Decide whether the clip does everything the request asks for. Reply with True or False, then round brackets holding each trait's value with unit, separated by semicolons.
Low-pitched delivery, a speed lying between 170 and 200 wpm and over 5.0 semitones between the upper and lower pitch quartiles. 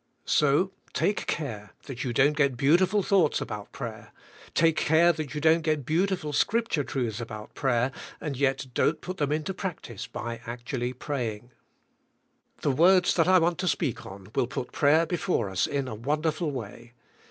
False (145 Hz; 175 wpm; 5.5 semitones)